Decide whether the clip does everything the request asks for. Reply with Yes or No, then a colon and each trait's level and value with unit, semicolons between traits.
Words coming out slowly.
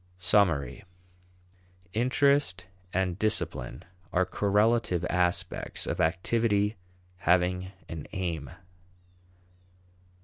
Yes: slow, 70 wpm